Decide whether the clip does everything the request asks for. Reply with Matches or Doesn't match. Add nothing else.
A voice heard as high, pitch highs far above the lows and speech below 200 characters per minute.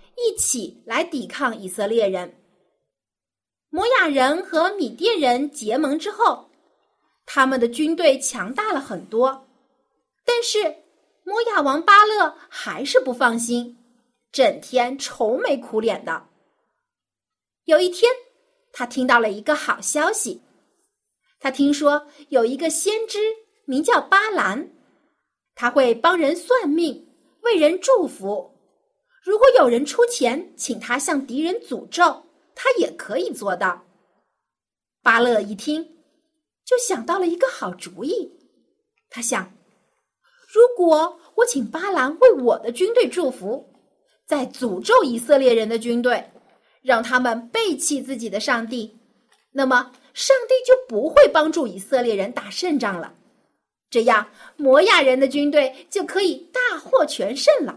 Matches